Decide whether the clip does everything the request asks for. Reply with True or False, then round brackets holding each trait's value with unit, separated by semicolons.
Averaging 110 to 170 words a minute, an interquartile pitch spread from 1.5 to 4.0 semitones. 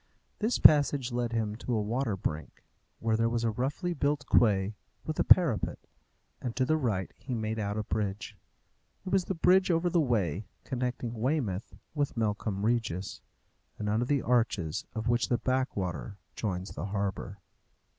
False (165 wpm; 4.5 semitones)